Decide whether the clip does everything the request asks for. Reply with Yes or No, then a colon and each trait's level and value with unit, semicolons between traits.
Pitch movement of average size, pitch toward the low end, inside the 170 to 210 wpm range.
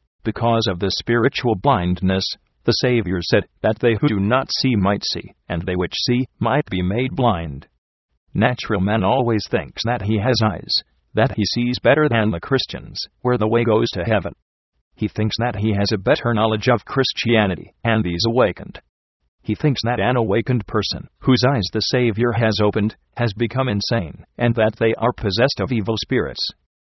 Yes: average, 3.8 semitones; low, 110 Hz; average, 180 wpm